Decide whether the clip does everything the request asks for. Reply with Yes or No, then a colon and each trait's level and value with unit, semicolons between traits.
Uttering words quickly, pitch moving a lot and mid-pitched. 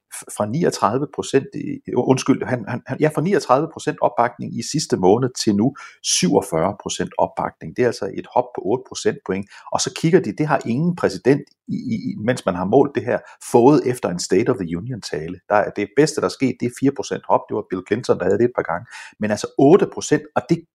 No: fast, 230 wpm; wide, 5.8 semitones; low, 130 Hz